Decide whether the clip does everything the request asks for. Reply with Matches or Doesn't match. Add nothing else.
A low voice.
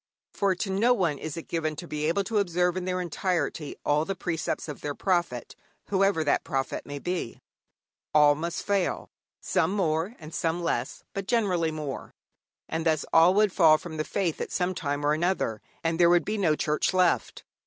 Doesn't match